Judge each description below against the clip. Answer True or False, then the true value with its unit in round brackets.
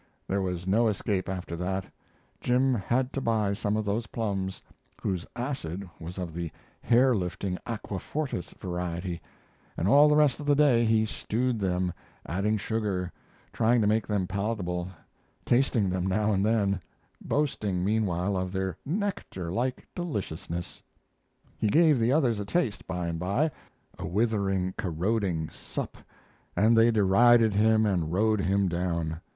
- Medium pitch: False (100 Hz)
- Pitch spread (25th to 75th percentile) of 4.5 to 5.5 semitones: False (4.1 semitones)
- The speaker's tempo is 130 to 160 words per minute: True (150 wpm)